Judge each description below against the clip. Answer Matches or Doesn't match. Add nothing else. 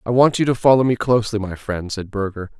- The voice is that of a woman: Doesn't match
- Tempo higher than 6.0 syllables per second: Matches